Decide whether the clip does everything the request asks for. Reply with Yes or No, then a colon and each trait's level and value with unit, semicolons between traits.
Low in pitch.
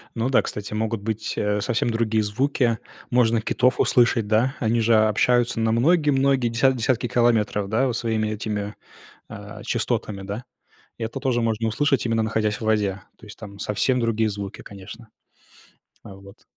Yes: low, 115 Hz